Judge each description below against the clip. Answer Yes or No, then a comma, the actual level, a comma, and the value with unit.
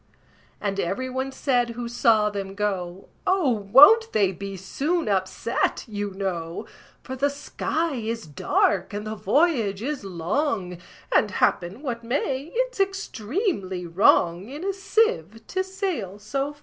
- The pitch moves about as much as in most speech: No, wide, 6.8 semitones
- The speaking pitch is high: Yes, high, 225 Hz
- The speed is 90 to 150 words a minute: Yes, average, 145 wpm